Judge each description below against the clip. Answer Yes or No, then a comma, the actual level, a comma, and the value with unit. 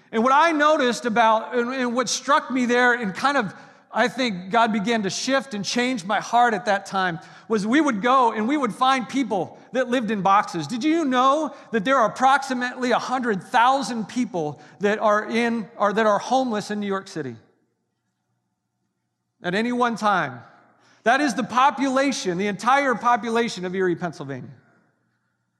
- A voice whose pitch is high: Yes, high, 230 Hz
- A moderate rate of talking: Yes, average, 170 wpm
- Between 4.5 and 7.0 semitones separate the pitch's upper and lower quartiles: Yes, average, 4.8 semitones